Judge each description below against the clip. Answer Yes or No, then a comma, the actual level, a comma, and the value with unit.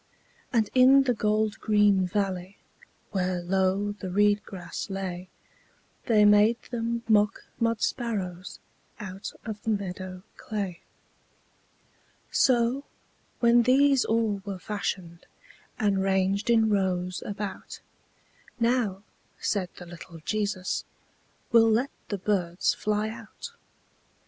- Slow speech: Yes, slow, 110 wpm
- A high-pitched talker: Yes, high, 205 Hz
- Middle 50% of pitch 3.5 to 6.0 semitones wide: No, average, 3.1 semitones